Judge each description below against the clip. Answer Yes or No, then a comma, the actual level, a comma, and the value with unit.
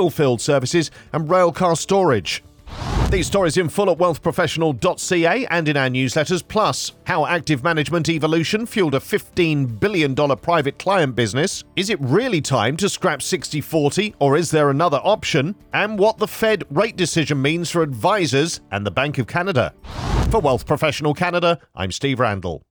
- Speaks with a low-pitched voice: No, medium, 160 Hz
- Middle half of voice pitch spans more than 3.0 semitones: Yes, average, 4.1 semitones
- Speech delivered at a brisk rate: No, average, 165 wpm